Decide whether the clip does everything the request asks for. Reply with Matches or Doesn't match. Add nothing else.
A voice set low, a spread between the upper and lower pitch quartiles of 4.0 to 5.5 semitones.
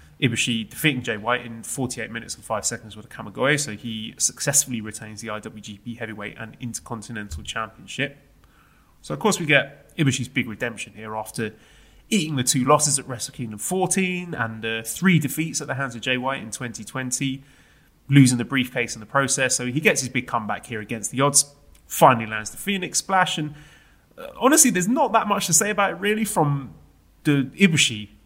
Matches